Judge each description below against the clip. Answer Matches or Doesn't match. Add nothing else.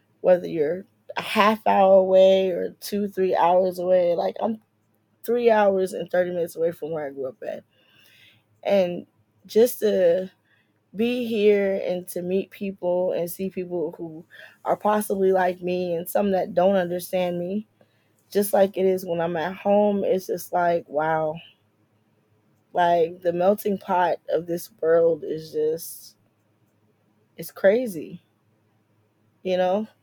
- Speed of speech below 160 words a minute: Matches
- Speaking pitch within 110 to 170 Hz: Doesn't match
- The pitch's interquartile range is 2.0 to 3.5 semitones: Doesn't match